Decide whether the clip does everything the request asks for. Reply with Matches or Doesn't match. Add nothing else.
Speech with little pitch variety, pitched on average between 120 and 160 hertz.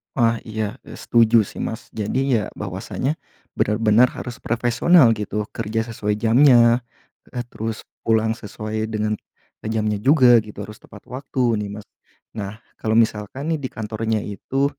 Doesn't match